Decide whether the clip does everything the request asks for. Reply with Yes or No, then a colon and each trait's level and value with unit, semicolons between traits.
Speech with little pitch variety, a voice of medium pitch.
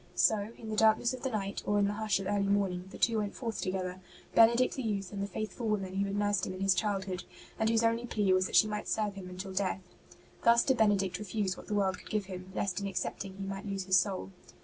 No: narrow, 2.2 semitones; high, 200 Hz